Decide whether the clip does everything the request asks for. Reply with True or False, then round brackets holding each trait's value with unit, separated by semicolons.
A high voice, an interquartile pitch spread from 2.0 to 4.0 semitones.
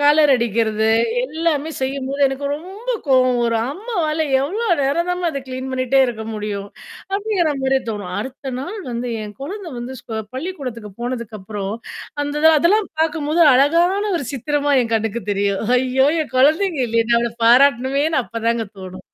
False (265 Hz; 5.3 semitones)